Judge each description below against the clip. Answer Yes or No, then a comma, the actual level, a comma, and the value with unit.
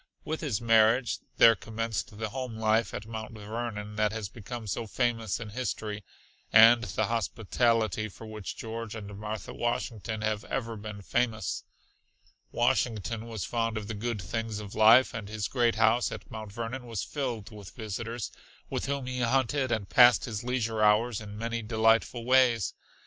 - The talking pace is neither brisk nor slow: Yes, average, 165 wpm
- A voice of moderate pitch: No, low, 115 Hz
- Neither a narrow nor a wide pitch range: No, narrow, 1.8 semitones